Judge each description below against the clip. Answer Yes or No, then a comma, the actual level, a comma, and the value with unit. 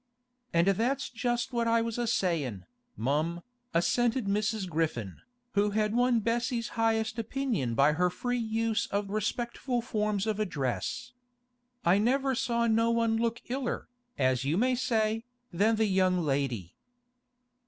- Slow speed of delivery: No, average, 145 wpm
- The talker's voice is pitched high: Yes, high, 220 Hz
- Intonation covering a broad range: No, average, 5.0 semitones